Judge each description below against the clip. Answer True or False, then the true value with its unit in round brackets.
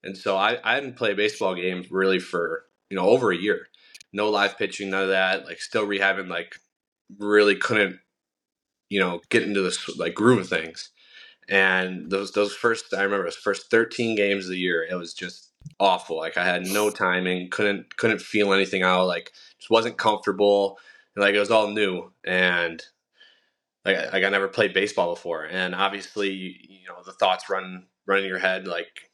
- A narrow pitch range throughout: True (1.8 semitones)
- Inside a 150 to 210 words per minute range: True (195 wpm)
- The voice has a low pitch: True (95 Hz)